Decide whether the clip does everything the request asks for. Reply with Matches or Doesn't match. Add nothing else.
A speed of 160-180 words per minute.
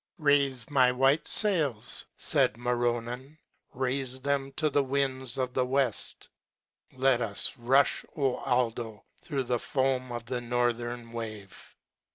Doesn't match